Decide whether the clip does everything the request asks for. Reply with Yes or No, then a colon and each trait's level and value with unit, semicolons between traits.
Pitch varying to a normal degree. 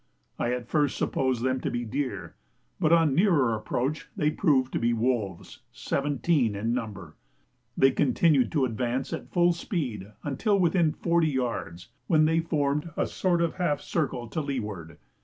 Yes: average, 5.0 semitones